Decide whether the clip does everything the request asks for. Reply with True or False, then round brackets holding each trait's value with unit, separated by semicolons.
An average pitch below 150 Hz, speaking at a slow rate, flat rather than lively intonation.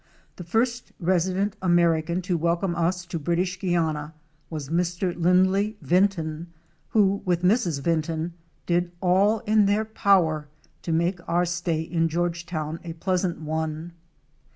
False (175 Hz; 130 wpm; 2.2 semitones)